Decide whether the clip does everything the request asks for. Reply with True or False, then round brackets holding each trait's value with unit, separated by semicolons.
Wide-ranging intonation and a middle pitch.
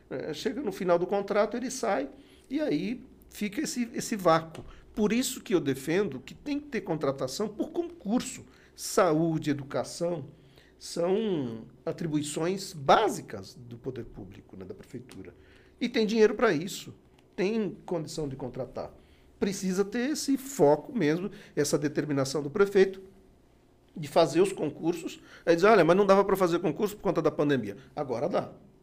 True (6.9 semitones; 180 Hz)